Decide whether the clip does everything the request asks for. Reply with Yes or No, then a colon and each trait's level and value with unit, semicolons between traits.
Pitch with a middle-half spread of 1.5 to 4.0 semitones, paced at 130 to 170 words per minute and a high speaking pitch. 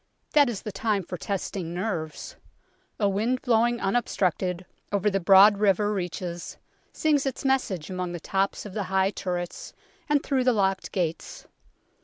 Yes: average, 3.6 semitones; average, 160 wpm; high, 195 Hz